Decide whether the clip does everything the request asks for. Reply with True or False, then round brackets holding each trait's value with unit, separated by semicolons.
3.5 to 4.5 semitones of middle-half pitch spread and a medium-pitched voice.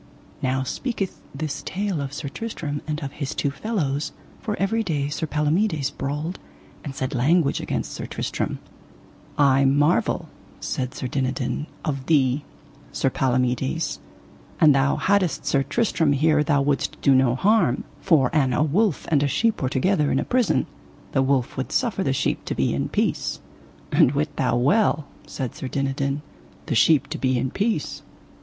True (3.8 semitones; 145 Hz)